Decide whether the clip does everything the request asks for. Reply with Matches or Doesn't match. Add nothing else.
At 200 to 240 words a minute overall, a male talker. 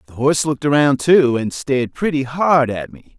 Matches